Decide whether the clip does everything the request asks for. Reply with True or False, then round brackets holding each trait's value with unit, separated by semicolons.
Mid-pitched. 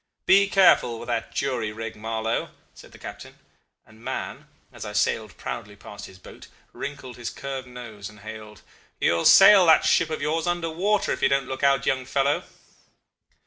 False (130 Hz)